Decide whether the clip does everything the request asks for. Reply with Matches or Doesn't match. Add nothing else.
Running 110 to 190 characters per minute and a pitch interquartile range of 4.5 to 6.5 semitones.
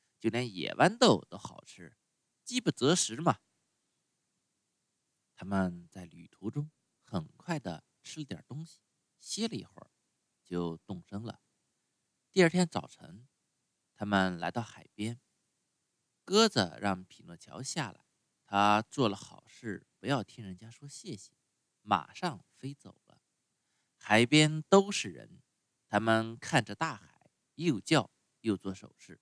Doesn't match